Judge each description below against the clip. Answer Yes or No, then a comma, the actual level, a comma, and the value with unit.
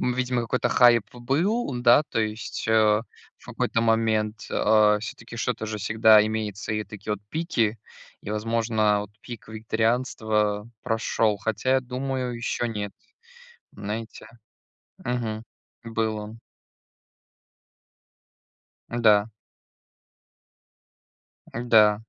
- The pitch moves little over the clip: Yes, narrow, 1.9 semitones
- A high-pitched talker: No, low, 110 Hz